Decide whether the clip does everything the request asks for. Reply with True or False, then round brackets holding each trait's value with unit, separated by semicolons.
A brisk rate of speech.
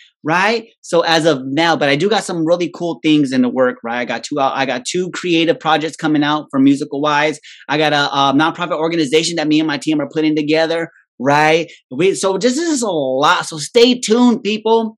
True (225 wpm)